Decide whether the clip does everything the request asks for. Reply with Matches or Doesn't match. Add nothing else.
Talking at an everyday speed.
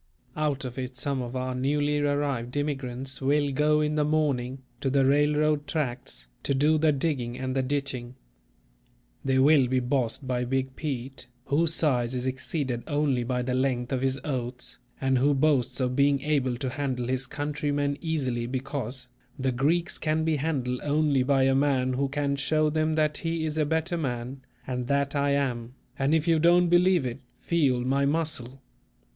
Matches